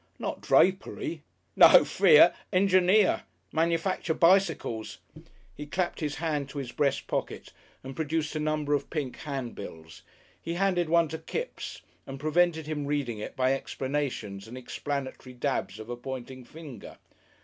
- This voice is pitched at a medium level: Yes, medium, 145 Hz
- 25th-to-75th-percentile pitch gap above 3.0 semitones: Yes, average, 4.1 semitones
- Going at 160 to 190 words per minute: No, average, 140 wpm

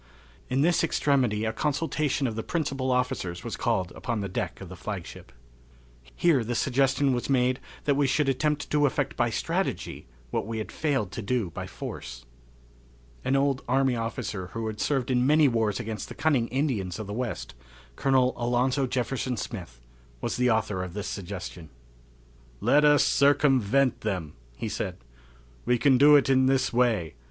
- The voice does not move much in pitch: No, average, 4.2 semitones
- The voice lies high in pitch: No, low, 125 Hz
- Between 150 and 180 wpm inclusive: Yes, average, 170 wpm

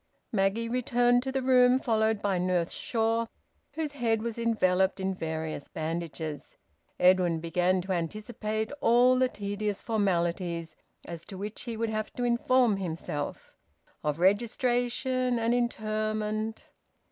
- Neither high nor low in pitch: No, high, 215 Hz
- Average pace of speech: No, slow, 130 wpm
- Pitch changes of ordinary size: Yes, average, 4.7 semitones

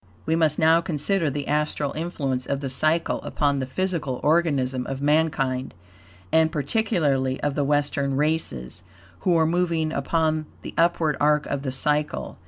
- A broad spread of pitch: No, average, 2.8 semitones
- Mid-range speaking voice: Yes, medium, 150 Hz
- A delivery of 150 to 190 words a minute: Yes, average, 155 wpm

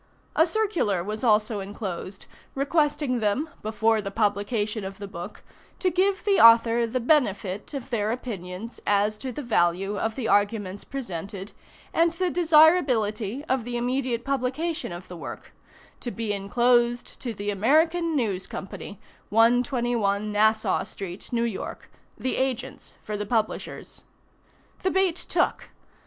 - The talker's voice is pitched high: Yes, high, 230 Hz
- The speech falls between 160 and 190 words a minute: No, average, 140 wpm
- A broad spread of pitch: No, average, 4.7 semitones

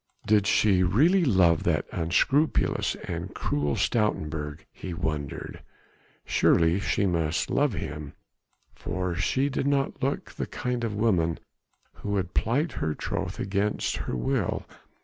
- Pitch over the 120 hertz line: No, very low, 95 Hz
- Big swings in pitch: Yes, wide, 6.1 semitones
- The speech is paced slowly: Yes, slow, 130 wpm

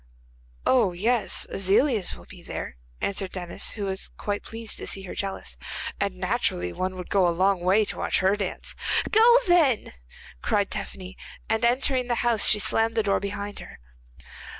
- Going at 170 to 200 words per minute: Yes, average, 175 wpm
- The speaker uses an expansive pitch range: No, average, 3.4 semitones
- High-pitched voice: Yes, high, 200 Hz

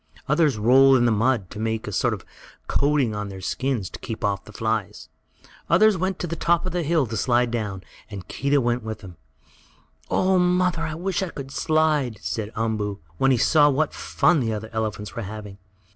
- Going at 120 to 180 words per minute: No, fast, 205 wpm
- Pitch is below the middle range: Yes, low, 120 Hz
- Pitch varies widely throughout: Yes, wide, 6.5 semitones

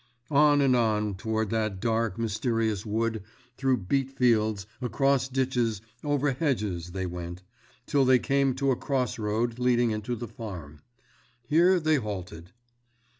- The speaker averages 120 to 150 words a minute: Yes, average, 140 wpm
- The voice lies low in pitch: Yes, low, 115 Hz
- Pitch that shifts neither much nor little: Yes, average, 4.0 semitones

